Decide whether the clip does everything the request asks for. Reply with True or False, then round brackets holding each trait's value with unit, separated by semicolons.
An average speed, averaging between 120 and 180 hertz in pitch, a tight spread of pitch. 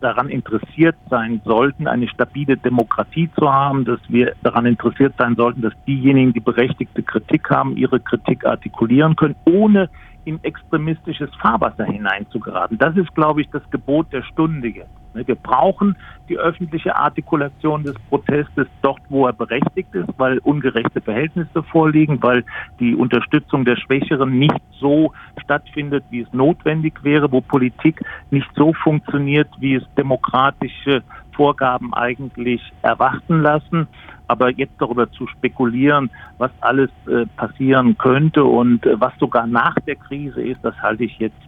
False (145 wpm; 135 Hz; 3.8 semitones)